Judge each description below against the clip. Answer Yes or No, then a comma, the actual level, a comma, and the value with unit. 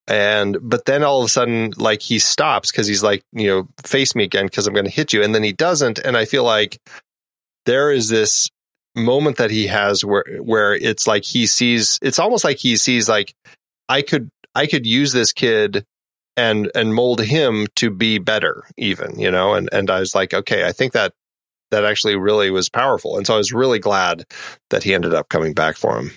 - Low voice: Yes, low, 105 Hz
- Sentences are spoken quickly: Yes, fast, 220 wpm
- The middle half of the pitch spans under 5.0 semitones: Yes, average, 2.8 semitones